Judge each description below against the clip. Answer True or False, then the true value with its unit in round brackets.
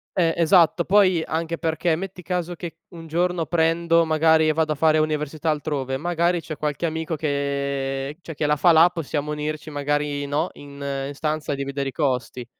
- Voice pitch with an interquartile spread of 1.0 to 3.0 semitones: True (2.5 semitones)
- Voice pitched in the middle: True (155 Hz)